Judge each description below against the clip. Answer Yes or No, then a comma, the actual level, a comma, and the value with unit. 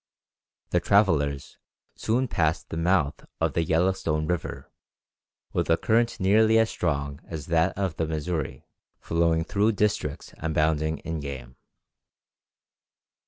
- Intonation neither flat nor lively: Yes, average, 3.8 semitones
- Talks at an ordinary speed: No, slow, 120 wpm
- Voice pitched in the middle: No, very low, 80 Hz